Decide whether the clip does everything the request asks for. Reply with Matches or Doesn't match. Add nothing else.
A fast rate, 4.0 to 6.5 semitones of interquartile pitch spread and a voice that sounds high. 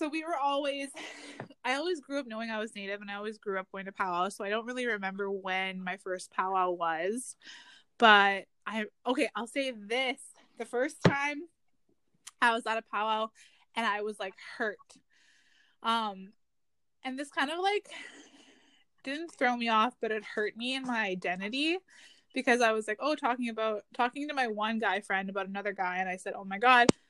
Doesn't match